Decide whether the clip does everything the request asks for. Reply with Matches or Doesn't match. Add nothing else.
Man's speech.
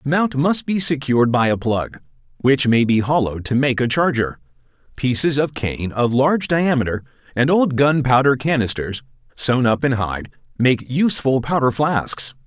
Matches